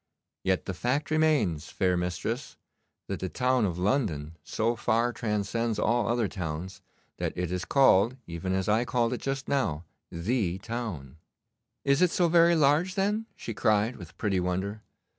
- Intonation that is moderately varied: No, wide, 6.1 semitones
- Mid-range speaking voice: No, low, 110 Hz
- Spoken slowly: No, average, 160 wpm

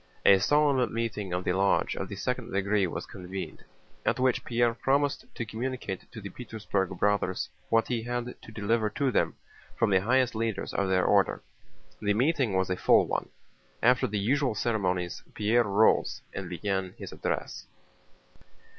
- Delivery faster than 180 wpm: No, average, 165 wpm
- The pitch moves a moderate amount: Yes, average, 3.9 semitones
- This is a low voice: Yes, low, 110 Hz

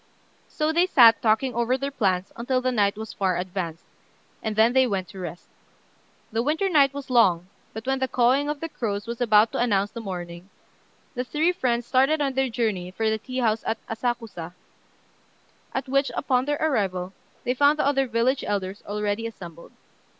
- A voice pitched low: No, high, 235 Hz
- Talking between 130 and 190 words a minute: Yes, average, 185 wpm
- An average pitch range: Yes, average, 4.7 semitones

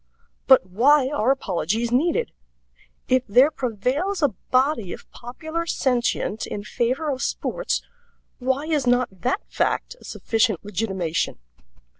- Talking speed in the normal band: No, slow, 125 wpm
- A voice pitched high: Yes, very high, 250 Hz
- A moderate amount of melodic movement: Yes, average, 5.0 semitones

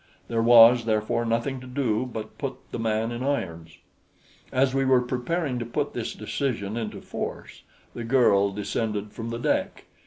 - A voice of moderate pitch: No, low, 115 Hz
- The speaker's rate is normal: Yes, average, 165 wpm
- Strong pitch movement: No, average, 2.8 semitones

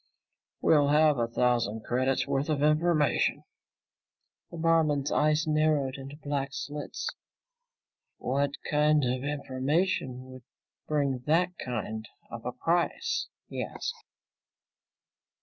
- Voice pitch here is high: No, medium, 145 Hz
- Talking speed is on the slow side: Yes, slow, 110 wpm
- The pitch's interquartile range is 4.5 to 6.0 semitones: No, average, 2.9 semitones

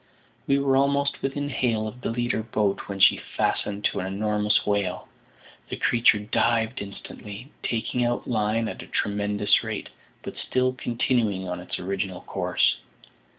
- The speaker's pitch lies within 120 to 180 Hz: No, low, 110 Hz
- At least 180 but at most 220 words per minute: No, average, 150 wpm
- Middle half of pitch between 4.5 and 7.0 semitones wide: No, average, 3.2 semitones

